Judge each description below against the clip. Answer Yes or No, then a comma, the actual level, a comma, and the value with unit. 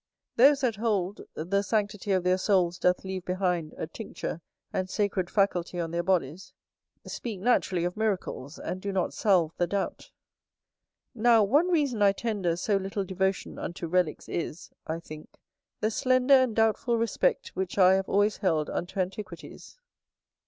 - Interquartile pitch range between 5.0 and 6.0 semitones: No, average, 3.4 semitones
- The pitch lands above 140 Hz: Yes, high, 190 Hz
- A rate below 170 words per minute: Yes, average, 160 wpm